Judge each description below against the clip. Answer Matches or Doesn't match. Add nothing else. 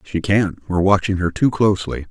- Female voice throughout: Doesn't match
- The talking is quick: Doesn't match